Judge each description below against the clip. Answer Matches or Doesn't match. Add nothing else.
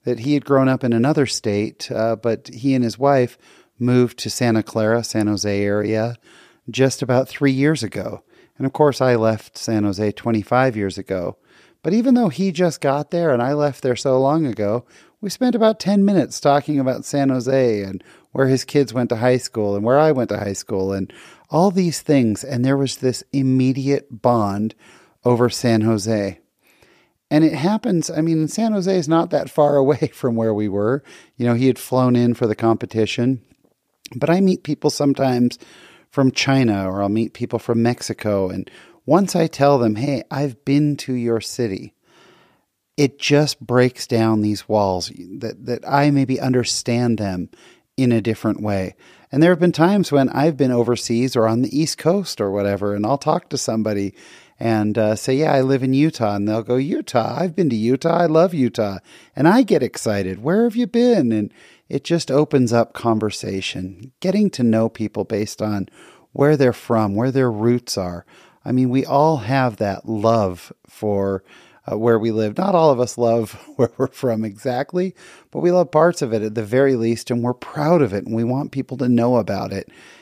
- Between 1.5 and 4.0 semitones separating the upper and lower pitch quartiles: Doesn't match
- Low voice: Matches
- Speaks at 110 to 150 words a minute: Doesn't match